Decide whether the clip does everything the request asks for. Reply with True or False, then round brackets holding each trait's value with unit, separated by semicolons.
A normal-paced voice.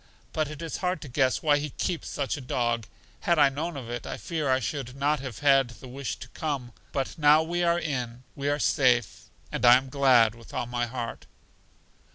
False (215 wpm)